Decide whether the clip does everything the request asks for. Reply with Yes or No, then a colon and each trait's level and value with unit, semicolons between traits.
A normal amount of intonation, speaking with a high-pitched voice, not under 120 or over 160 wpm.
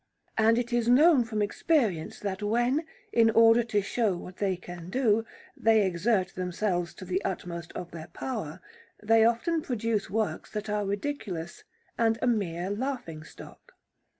Yes: average, 4.3 semitones; high, 210 Hz; average, 155 wpm